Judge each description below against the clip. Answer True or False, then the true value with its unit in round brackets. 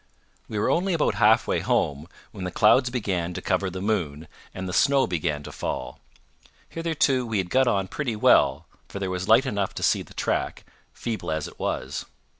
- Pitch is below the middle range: True (100 Hz)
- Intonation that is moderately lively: False (5.8 semitones)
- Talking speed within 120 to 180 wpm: False (195 wpm)